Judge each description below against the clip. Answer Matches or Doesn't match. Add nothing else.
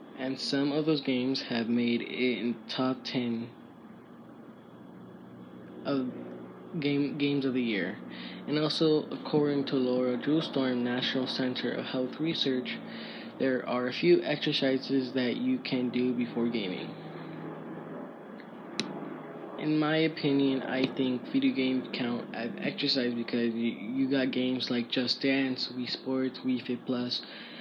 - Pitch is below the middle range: Matches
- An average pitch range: Doesn't match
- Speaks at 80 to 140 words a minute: Matches